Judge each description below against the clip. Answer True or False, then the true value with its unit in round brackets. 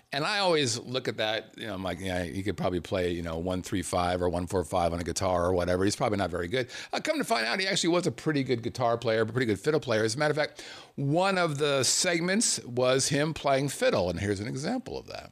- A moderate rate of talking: False (285 wpm)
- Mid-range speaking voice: False (115 Hz)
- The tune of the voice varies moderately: False (8.5 semitones)